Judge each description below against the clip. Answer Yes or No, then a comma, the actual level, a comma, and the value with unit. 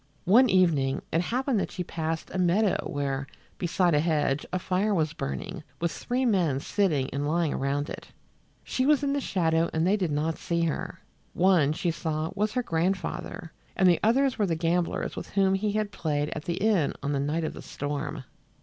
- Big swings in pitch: No, average, 4.4 semitones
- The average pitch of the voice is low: No, medium, 170 Hz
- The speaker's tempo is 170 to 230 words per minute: Yes, average, 200 wpm